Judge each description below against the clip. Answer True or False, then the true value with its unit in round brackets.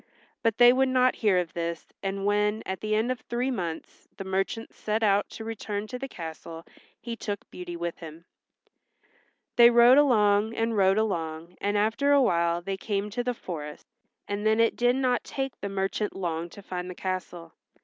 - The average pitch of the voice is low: False (205 Hz)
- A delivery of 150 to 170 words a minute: False (190 wpm)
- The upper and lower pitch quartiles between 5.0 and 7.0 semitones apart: False (4.4 semitones)